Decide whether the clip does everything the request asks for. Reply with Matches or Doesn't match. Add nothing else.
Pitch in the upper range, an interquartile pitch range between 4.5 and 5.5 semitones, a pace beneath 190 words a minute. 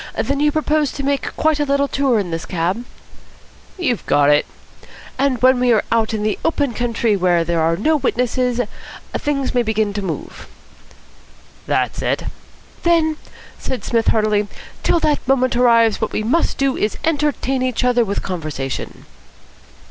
Matches